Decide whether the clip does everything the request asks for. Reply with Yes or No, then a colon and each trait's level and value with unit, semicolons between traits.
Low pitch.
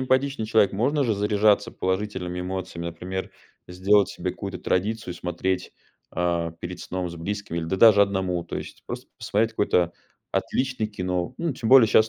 Yes: very low, 95 Hz